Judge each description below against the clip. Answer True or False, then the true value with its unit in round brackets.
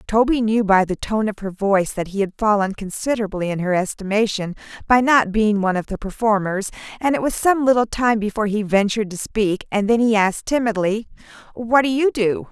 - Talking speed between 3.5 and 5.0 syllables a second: False (5.7 syllables/s)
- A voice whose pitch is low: False (215 Hz)